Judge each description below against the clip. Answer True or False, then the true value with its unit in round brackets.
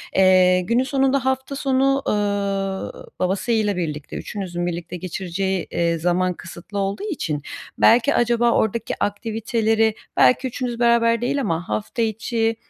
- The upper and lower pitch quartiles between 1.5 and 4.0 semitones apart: False (4.6 semitones)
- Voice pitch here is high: True (210 Hz)